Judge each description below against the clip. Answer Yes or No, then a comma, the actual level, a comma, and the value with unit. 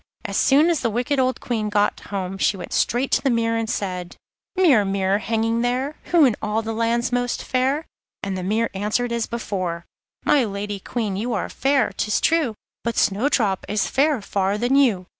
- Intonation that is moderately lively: Yes, average, 4.0 semitones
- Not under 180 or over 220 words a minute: Yes, average, 195 wpm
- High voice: Yes, high, 225 Hz